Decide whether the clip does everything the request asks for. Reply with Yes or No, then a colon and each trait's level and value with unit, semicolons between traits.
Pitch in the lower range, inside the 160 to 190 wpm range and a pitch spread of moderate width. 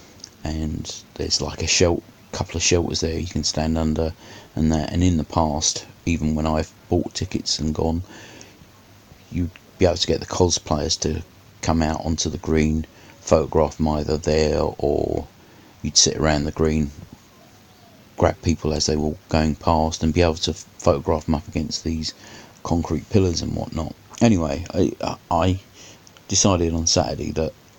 Yes: very low, 80 Hz; average, 165 wpm; average, 3.1 semitones